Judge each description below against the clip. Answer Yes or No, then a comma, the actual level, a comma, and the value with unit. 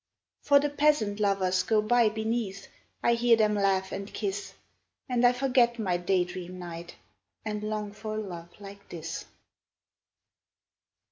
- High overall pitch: Yes, high, 210 Hz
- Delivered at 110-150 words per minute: Yes, average, 145 wpm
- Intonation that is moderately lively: Yes, average, 3.5 semitones